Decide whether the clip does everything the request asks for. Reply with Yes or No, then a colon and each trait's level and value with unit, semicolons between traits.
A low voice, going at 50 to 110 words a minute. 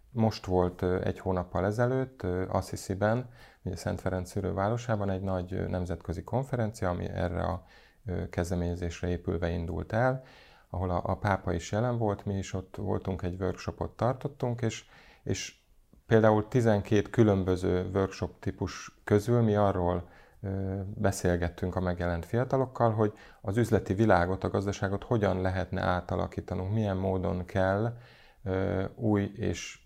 No: very low, 95 Hz; average, 125 wpm